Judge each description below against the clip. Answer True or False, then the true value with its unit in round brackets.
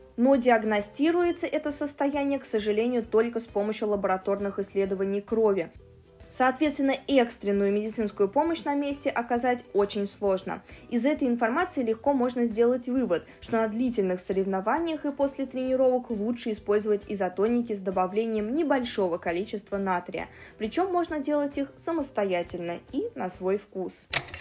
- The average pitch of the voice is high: True (225 Hz)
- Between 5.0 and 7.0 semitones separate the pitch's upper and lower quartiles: True (5.4 semitones)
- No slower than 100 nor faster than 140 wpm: True (130 wpm)